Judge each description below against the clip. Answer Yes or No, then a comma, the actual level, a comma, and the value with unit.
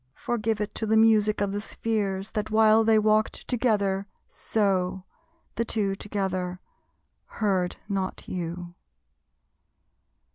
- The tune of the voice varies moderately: No, narrow, 2.3 semitones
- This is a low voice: No, high, 205 Hz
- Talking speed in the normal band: No, slow, 115 wpm